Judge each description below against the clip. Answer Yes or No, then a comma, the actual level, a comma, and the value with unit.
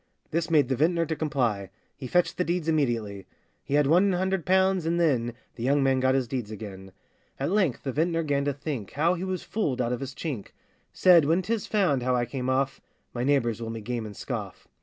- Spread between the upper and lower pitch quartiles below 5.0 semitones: No, wide, 5.6 semitones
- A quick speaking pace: Yes, fast, 225 wpm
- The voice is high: No, medium, 140 Hz